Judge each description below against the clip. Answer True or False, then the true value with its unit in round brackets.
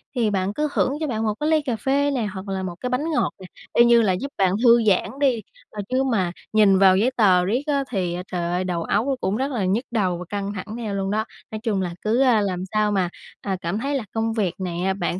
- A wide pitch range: False (4.7 semitones)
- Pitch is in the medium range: False (210 Hz)